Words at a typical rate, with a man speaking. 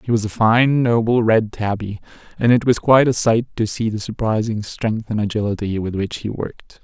No: fast, 210 wpm; male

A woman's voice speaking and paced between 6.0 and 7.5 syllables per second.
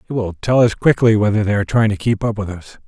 No: male; 6.5 syllables/s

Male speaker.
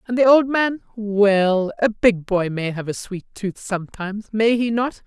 No: female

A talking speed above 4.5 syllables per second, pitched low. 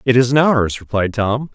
No: 4.3 syllables/s; low, 120 Hz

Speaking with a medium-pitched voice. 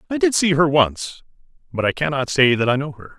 Yes: medium, 145 Hz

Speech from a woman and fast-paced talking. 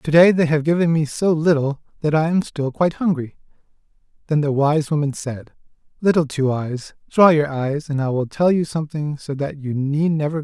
No: male; fast, 225 wpm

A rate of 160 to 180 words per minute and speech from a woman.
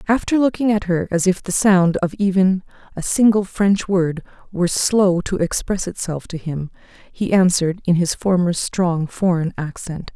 Yes: average, 170 wpm; female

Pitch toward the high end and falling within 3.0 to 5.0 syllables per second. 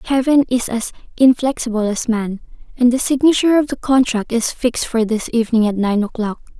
No: high, 240 Hz; 5.7 syllables/s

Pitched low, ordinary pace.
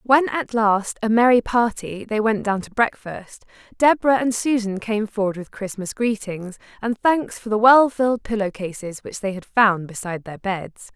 No: high, 215 Hz; average, 185 wpm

